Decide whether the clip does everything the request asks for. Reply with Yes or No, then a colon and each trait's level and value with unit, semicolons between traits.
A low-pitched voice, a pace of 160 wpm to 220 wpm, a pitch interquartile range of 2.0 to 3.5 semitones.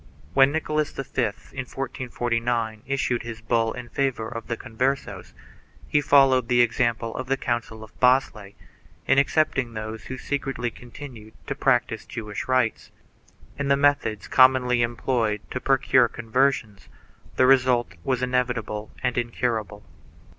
No: low, 125 Hz; average, 140 wpm; average, 2.7 semitones